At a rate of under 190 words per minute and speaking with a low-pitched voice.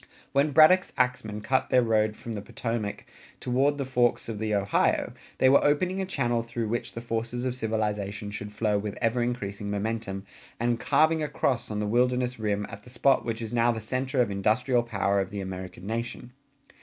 No: average, 195 wpm; low, 115 Hz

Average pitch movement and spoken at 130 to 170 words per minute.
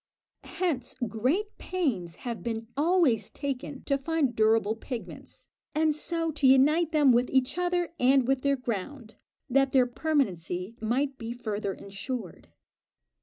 Yes: average, 4.9 semitones; slow, 135 wpm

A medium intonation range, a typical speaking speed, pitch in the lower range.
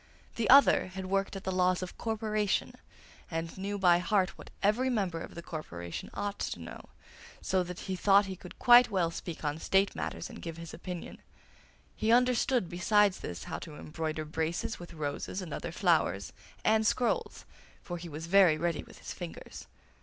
No: average, 3.5 semitones; average, 185 wpm; medium, 185 Hz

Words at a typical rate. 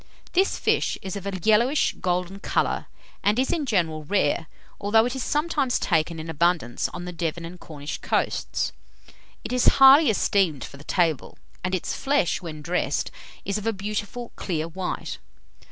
Yes: average, 170 wpm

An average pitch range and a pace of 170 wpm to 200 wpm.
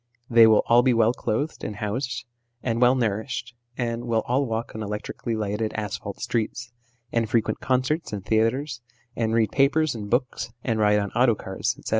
No: narrow, 2.3 semitones; average, 180 wpm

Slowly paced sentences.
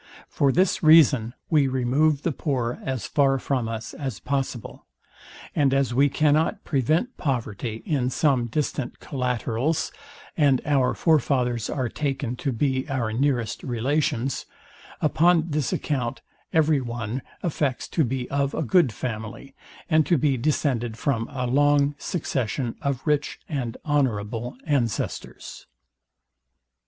Yes: slow, 130 wpm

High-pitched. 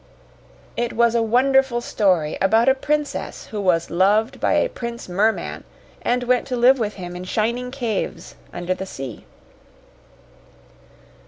Yes: high, 230 Hz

